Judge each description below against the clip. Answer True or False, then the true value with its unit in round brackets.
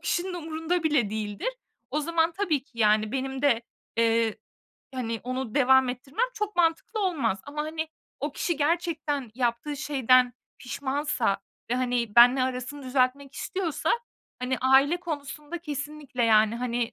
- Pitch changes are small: False (4.3 semitones)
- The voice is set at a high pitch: True (270 Hz)